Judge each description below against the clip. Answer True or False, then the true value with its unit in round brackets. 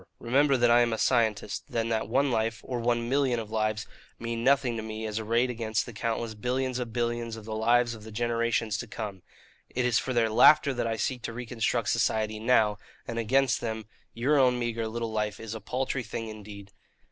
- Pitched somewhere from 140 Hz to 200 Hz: False (115 Hz)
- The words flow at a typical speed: False (210 wpm)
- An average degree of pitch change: False (1.9 semitones)